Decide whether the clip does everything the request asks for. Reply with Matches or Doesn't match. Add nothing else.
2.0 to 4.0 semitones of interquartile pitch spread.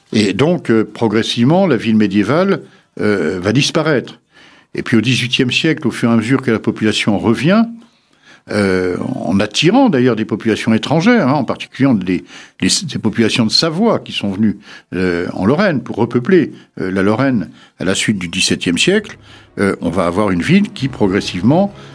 Doesn't match